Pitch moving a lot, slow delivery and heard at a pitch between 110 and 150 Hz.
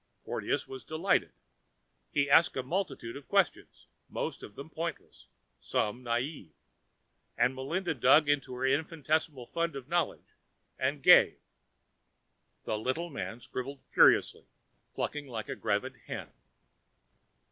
No: average, 4.1 semitones; slow, 125 wpm; medium, 140 Hz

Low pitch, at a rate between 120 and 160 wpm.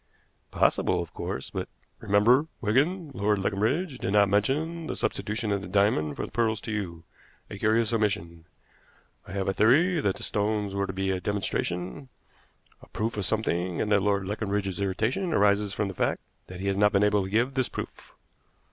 No: low, 105 Hz; average, 190 wpm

